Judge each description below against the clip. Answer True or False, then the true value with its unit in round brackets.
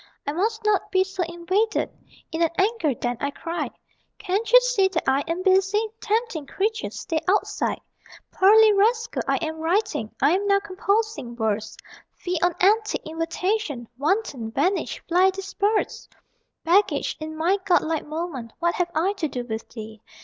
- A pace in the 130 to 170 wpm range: True (155 wpm)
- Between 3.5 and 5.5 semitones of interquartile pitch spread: True (4.8 semitones)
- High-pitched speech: True (365 Hz)